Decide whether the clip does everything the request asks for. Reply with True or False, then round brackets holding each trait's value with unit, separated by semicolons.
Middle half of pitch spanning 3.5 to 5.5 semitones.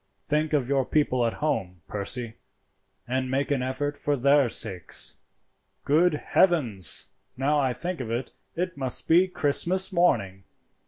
True (4.3 semitones)